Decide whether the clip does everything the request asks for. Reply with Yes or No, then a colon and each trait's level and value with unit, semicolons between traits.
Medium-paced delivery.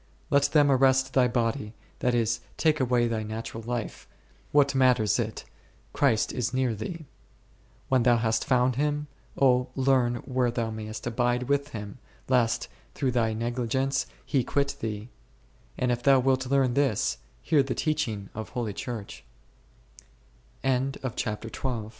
No: slow, 130 wpm